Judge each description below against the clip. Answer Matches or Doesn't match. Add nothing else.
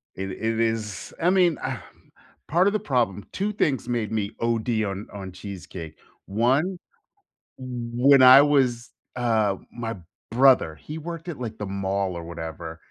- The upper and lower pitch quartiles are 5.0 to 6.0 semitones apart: Matches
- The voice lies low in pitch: Matches